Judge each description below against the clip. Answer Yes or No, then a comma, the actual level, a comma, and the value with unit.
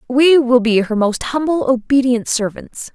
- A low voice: No, very high, 250 Hz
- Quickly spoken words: No, average, 165 wpm